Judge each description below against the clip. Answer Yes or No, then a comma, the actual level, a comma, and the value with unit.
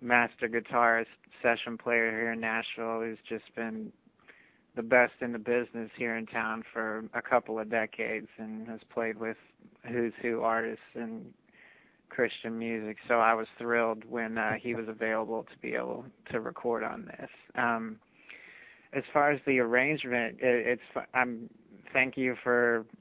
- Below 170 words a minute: Yes, average, 160 wpm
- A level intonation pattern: Yes, narrow, 1.3 semitones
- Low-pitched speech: Yes, low, 115 Hz